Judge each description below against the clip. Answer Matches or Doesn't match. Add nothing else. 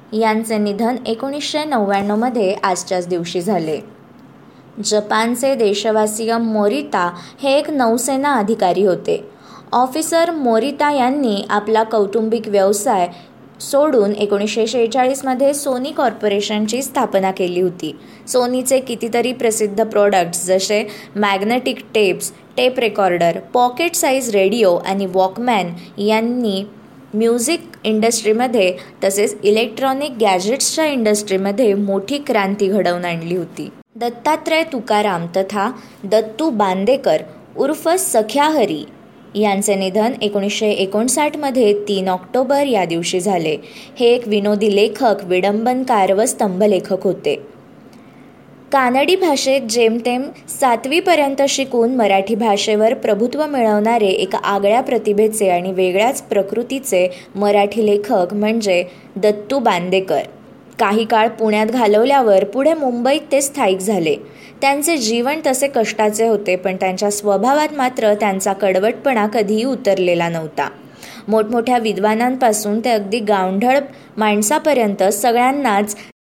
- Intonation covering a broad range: Doesn't match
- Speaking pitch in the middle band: Doesn't match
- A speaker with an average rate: Matches